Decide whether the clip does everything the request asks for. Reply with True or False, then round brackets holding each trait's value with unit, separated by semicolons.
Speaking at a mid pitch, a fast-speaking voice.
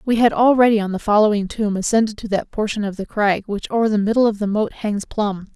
False (210 Hz; 250 wpm)